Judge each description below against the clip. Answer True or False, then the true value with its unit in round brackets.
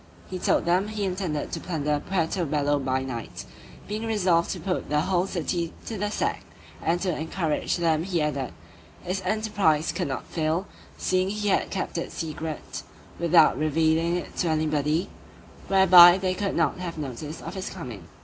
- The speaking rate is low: False (170 wpm)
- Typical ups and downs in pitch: True (3.6 semitones)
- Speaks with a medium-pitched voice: True (170 Hz)